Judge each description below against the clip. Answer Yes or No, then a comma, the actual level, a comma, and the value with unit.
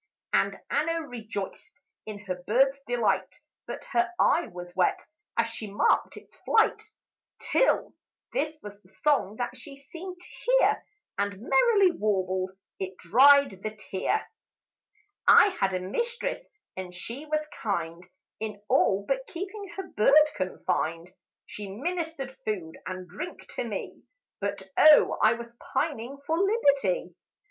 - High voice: Yes, high, 235 Hz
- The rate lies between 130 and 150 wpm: Yes, slow, 135 wpm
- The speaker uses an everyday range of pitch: No, wide, 8.5 semitones